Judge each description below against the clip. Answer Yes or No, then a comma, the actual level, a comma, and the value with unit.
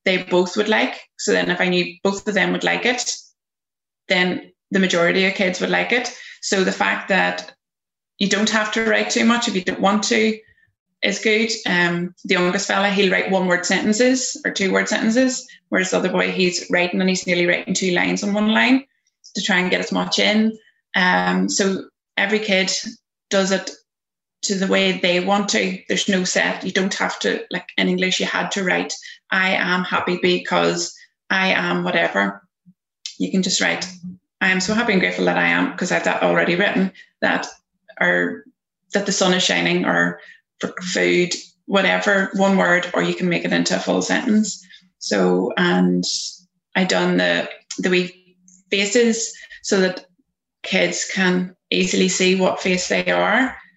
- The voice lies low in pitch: No, medium, 185 Hz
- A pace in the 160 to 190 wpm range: Yes, average, 185 wpm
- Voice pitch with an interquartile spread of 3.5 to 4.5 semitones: No, narrow, 2.4 semitones